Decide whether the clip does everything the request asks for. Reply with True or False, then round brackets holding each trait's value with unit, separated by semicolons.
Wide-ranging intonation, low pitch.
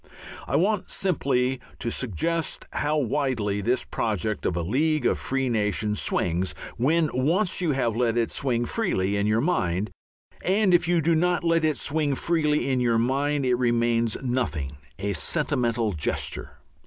True (6.1 semitones; 125 Hz)